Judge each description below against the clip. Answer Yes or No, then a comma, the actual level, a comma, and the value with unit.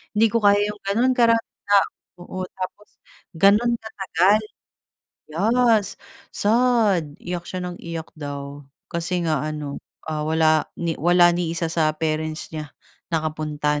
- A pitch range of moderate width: Yes, average, 4.8 semitones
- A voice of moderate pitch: Yes, medium, 175 Hz